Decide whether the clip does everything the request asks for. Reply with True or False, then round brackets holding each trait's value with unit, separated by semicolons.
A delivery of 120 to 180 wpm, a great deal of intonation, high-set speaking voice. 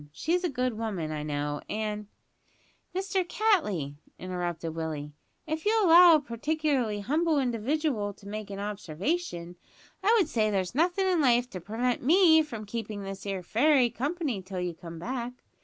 True (165 wpm; 8.7 semitones; 230 Hz)